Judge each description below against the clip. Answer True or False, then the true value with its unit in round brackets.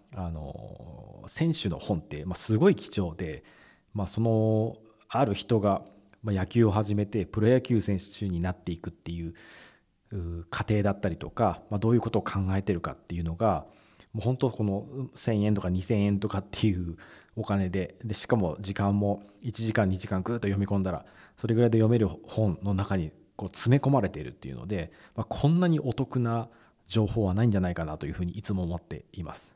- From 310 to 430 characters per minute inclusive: True (355 characters per minute)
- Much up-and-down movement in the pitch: False (3.5 semitones)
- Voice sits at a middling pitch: False (100 Hz)